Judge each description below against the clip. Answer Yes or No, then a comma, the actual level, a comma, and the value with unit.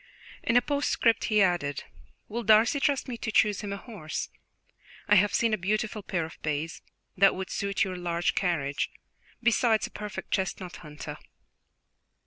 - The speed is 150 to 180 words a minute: Yes, average, 160 wpm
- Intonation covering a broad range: No, average, 4.0 semitones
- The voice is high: Yes, high, 200 Hz